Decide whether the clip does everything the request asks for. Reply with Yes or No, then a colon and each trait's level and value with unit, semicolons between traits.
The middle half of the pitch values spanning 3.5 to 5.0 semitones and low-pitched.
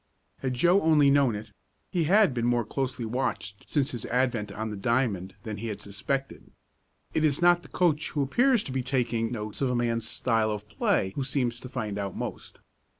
Yes: average, 4.3 semitones; low, 125 Hz